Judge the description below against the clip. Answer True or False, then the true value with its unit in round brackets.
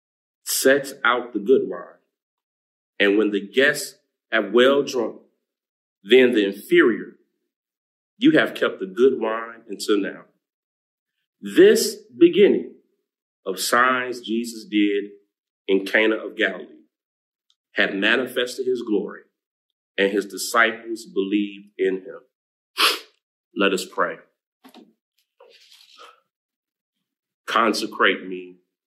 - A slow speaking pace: True (100 wpm)